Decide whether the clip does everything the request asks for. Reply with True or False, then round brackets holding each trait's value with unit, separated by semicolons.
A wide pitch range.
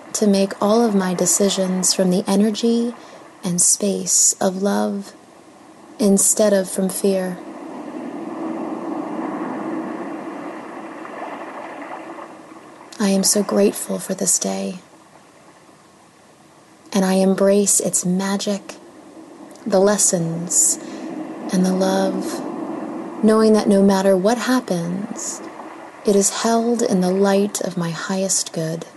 True (8.4 semitones)